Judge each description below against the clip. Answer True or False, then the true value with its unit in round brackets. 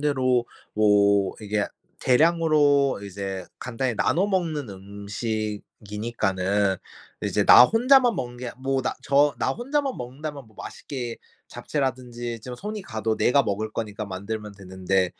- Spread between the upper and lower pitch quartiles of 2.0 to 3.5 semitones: False (5.6 semitones)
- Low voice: True (120 Hz)